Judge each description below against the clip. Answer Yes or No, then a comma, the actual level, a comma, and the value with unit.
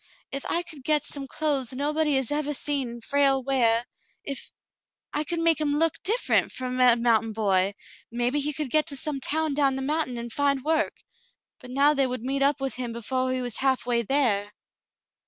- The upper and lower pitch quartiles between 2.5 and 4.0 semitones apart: Yes, average, 3.2 semitones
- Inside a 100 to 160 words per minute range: No, average, 200 wpm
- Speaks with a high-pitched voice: Yes, very high, 270 Hz